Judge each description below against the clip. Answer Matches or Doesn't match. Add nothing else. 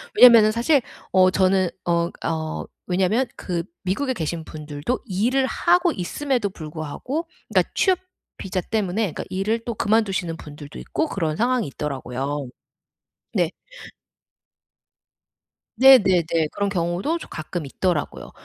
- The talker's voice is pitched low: Doesn't match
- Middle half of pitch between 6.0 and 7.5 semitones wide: Matches